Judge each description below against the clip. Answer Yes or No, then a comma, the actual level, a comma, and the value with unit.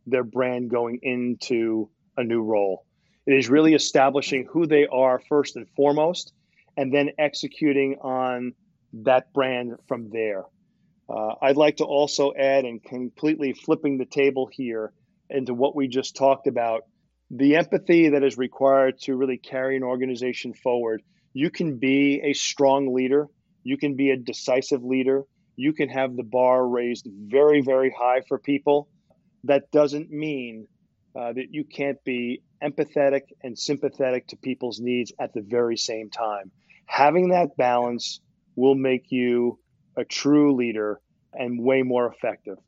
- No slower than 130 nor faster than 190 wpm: Yes, average, 155 wpm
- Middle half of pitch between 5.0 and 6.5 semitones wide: No, average, 2.7 semitones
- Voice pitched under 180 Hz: Yes, low, 135 Hz